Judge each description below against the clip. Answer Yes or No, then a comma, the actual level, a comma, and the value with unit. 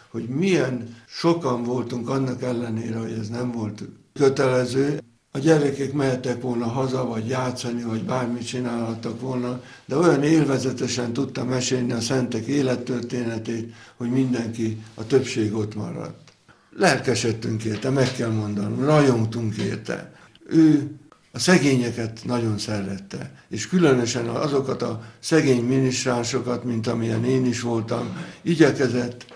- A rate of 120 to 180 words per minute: Yes, average, 125 wpm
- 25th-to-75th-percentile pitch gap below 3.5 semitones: Yes, narrow, 2.5 semitones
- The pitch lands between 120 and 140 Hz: Yes, low, 125 Hz